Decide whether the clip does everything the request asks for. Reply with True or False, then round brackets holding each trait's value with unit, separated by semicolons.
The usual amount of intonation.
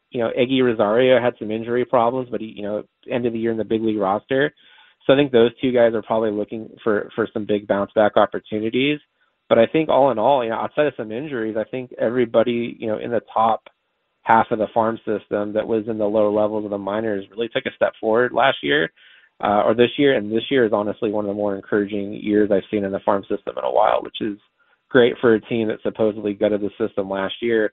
False (2.2 semitones)